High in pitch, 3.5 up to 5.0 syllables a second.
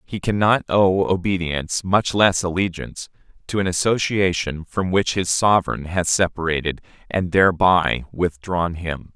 No: very low, 90 Hz; 4.6 syllables/s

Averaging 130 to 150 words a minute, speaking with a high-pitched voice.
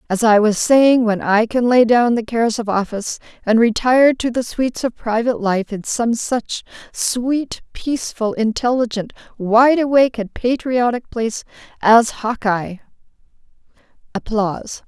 Yes: average, 140 wpm; high, 230 Hz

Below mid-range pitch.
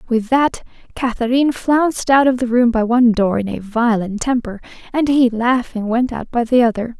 No: high, 240 Hz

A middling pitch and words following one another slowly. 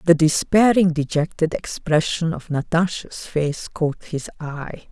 Yes: medium, 160 Hz; slow, 120 wpm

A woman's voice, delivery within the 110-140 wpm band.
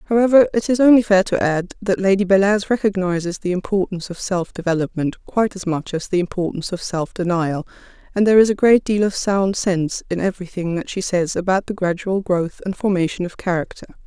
No: female; average, 200 wpm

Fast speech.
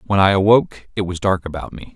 Yes: fast, 245 wpm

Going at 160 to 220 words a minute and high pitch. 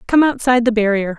Yes: average, 200 wpm; high, 235 Hz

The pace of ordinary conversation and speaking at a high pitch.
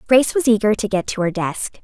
No: fast, 260 wpm; high, 215 Hz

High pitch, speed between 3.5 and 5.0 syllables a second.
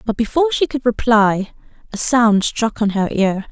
Yes: high, 225 Hz; 4.7 syllables/s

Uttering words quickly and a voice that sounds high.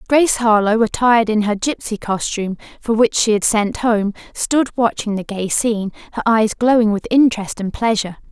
No: average, 180 wpm; high, 220 Hz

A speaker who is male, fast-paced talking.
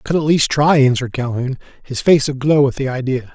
Yes: male; fast, 235 wpm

